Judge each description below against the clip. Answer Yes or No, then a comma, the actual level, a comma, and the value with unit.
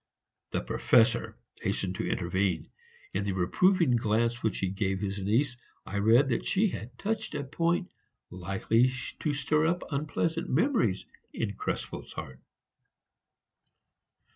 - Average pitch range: No, wide, 8.2 semitones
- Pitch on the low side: Yes, low, 115 Hz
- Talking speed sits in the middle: No, slow, 130 wpm